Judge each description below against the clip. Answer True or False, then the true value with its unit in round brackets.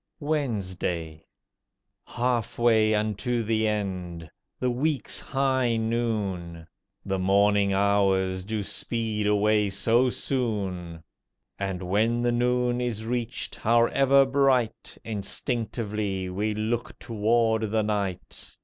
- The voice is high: False (110 Hz)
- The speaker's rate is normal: False (100 wpm)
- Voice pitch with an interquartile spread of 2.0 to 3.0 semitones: False (3.4 semitones)